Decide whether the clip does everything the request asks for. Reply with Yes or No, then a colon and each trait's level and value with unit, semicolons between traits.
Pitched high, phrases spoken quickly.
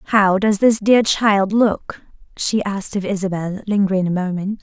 No: high, 200 Hz; average, 170 wpm